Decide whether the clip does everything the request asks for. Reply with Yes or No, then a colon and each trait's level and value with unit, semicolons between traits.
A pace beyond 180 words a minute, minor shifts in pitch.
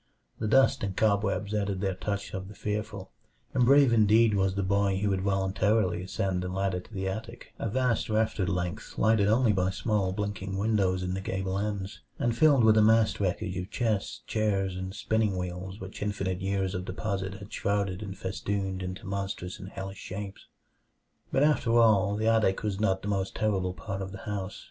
Yes: average, 190 wpm; narrow, 2.3 semitones